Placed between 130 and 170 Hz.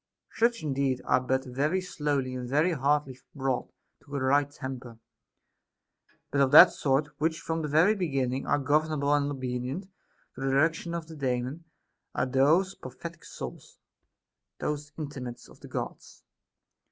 Yes: medium, 140 Hz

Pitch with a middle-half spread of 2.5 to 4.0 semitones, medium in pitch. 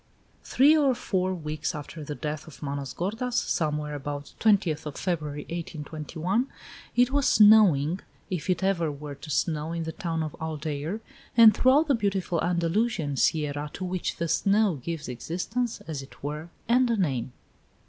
No: average, 5.3 semitones; medium, 165 Hz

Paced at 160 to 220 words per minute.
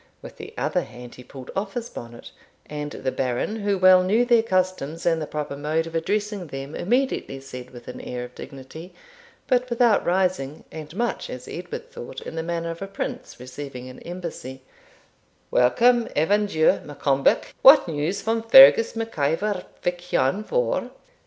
Yes: average, 170 wpm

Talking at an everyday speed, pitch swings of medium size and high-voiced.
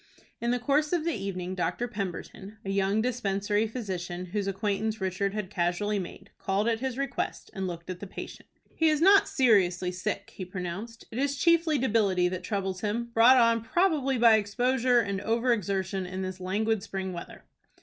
Yes: average, 180 wpm; average, 4.2 semitones; high, 205 Hz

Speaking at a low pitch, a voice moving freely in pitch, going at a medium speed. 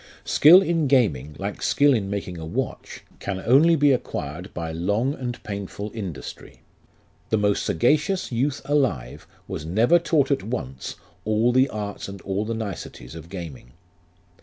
Yes: low, 105 Hz; wide, 6.7 semitones; average, 155 wpm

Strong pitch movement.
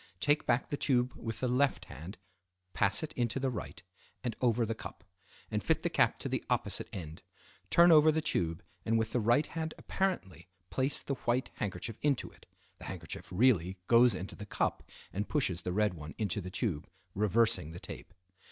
Yes: wide, 5.9 semitones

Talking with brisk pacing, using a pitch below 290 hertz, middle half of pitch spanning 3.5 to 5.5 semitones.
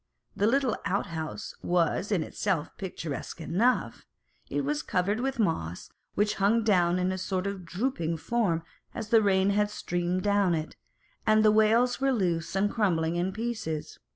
No: average, 160 wpm; high, 190 Hz; average, 4.2 semitones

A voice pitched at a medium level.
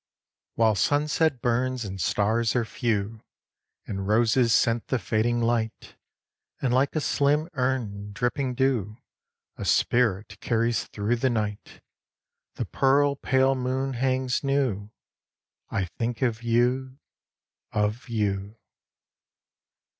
No: low, 120 Hz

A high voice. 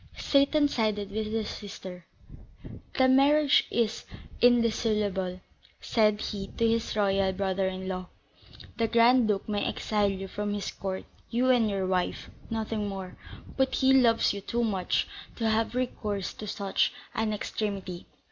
Yes: high, 210 Hz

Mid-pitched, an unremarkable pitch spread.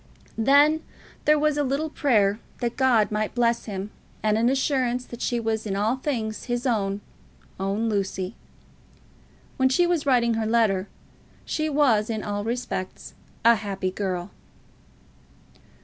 No: high, 230 Hz; average, 4.1 semitones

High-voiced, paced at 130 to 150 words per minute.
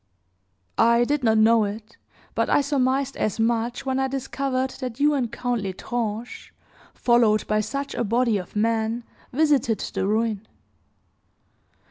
Yes: high, 235 Hz; average, 140 wpm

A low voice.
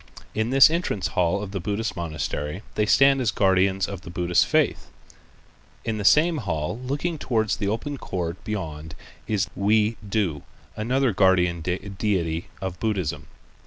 Yes: low, 100 Hz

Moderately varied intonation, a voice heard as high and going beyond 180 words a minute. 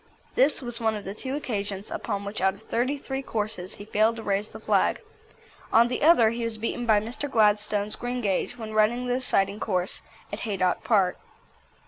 Yes: average, 3.0 semitones; high, 220 Hz; average, 190 wpm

